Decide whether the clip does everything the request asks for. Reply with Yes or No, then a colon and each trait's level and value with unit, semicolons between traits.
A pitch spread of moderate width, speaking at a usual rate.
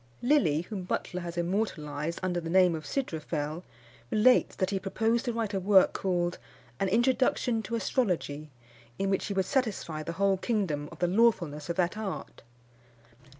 Yes: average, 4.6 semitones; average, 165 wpm